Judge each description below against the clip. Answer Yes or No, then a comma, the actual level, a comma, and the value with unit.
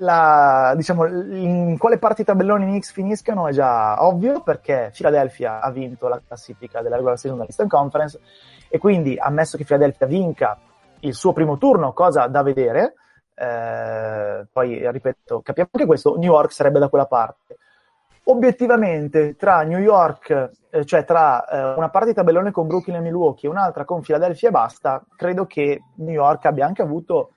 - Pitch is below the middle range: No, medium, 165 Hz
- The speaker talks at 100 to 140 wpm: No, average, 165 wpm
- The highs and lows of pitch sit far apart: Yes, wide, 6.3 semitones